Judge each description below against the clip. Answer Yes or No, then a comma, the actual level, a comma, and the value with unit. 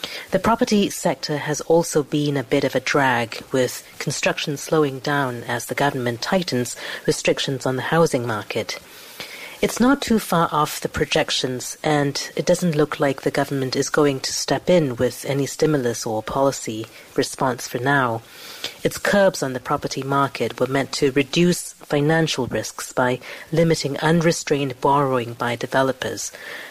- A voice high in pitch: No, medium, 140 Hz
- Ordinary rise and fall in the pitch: Yes, average, 3.4 semitones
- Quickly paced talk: No, average, 155 wpm